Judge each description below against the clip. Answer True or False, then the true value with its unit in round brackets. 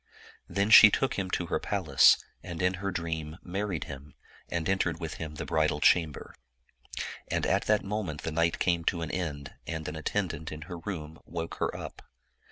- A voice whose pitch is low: True (85 Hz)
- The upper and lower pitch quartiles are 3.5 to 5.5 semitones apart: False (3.1 semitones)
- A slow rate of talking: False (185 wpm)